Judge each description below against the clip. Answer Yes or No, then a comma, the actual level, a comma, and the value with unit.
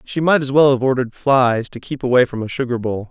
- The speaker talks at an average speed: No, fast, 270 wpm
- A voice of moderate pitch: No, low, 130 Hz